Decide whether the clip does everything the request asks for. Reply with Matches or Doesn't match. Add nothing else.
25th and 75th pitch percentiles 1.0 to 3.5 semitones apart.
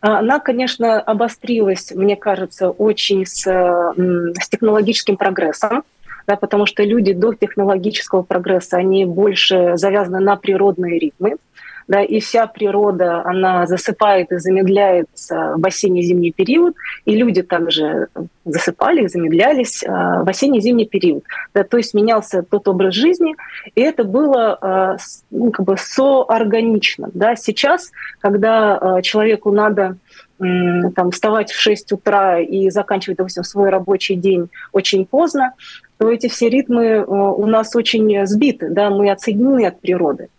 Matches